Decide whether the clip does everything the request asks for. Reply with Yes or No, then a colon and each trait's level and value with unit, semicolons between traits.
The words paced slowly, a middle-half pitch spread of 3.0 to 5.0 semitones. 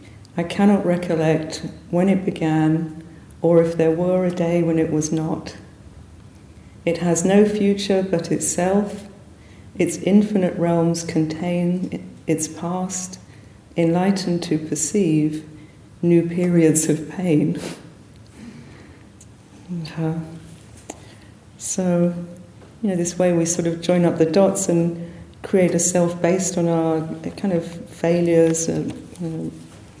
No: slow, 120 wpm; narrow, 2.4 semitones